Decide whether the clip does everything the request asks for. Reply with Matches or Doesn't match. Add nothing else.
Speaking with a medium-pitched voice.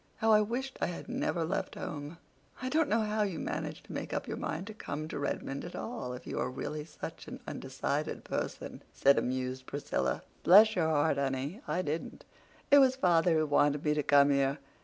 Matches